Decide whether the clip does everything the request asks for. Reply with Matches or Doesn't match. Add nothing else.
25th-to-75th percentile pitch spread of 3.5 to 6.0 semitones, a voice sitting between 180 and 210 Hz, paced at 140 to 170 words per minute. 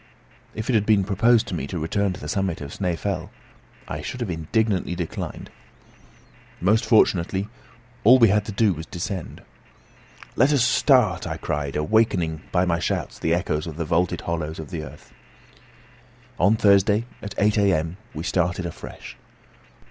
Doesn't match